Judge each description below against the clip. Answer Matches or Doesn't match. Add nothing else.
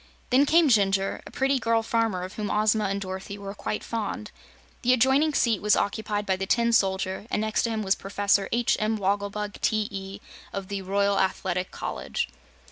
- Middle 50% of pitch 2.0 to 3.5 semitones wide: Matches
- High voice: Matches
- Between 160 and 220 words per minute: Matches